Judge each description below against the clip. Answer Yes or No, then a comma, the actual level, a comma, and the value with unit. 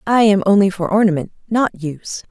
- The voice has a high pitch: Yes, high, 195 Hz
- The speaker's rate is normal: Yes, average, 180 wpm